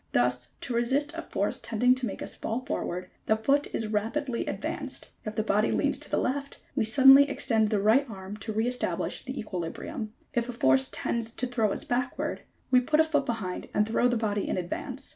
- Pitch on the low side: No, high, 230 Hz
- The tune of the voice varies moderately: Yes, average, 3.6 semitones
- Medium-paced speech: No, fast, 210 wpm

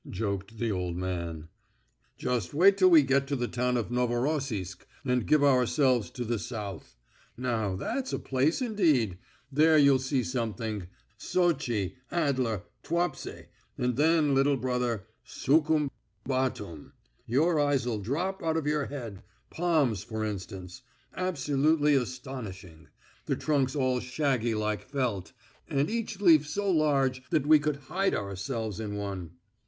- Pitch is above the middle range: No, low, 130 Hz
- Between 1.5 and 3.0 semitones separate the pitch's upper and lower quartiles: No, wide, 5.6 semitones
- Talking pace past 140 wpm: No, slow, 135 wpm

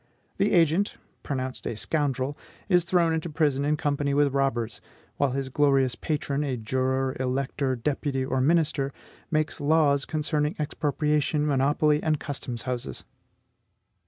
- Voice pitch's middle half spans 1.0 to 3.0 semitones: Yes, narrow, 2.5 semitones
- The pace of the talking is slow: Yes, slow, 130 wpm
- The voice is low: No, medium, 145 Hz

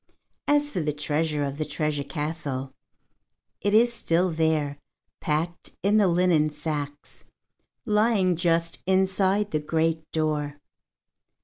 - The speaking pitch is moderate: Yes, medium, 160 Hz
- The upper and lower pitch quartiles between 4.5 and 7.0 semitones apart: No, average, 3.9 semitones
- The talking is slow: Yes, slow, 120 wpm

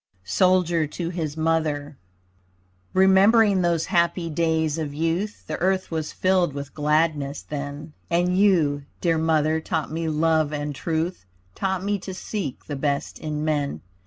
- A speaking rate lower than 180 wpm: Yes, average, 145 wpm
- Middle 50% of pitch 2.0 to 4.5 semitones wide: Yes, average, 3.2 semitones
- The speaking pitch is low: No, medium, 160 Hz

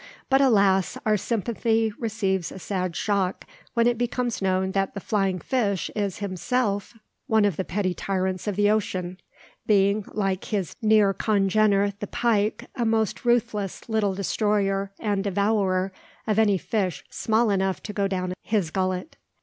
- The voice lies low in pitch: No, high, 200 Hz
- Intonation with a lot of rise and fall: No, narrow, 2.4 semitones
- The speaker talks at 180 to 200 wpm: No, average, 155 wpm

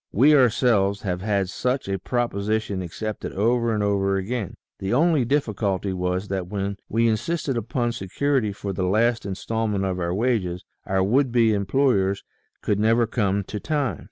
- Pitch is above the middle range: No, low, 105 Hz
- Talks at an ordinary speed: Yes, average, 165 wpm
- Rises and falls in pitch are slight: No, average, 3.8 semitones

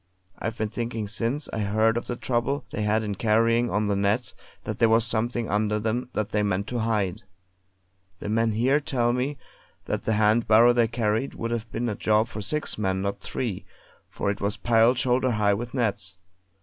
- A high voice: No, low, 110 Hz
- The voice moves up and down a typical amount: No, narrow, 2.2 semitones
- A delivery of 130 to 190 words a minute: No, average, 200 wpm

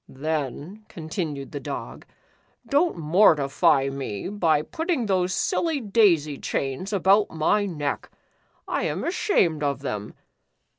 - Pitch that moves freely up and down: Yes, wide, 6.4 semitones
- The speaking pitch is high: No, medium, 160 Hz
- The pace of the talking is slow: Yes, slow, 115 wpm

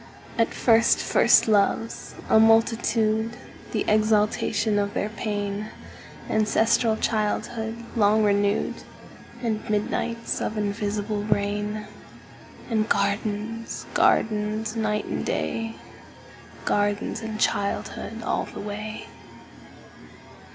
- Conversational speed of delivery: No, slow, 80 wpm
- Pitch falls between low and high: No, high, 215 Hz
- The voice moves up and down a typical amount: No, narrow, 1.4 semitones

